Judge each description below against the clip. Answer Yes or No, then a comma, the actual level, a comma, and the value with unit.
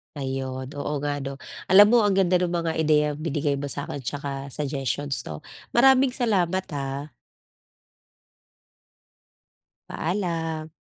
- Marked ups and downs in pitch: No, average, 4.3 semitones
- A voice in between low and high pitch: Yes, medium, 150 Hz